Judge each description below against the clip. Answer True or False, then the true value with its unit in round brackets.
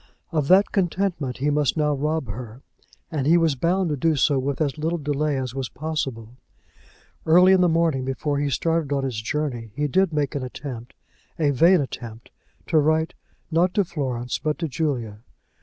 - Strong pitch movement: False (3.7 semitones)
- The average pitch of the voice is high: False (150 Hz)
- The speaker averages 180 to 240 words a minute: True (185 wpm)